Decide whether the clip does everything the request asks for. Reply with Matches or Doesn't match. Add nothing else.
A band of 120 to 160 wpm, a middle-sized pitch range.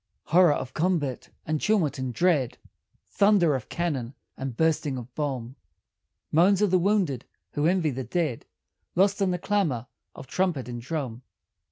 Doesn't match